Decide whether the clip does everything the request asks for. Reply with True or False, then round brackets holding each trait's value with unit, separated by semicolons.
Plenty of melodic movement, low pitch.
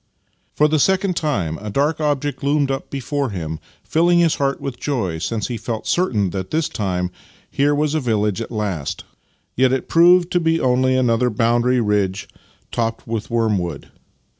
True (5.9 semitones; 125 Hz)